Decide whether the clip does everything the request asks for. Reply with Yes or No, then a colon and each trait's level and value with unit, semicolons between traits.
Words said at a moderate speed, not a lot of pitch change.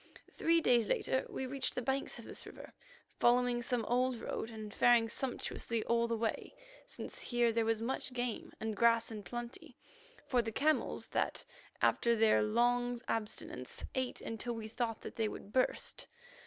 Yes: average, 170 wpm; narrow, 1.7 semitones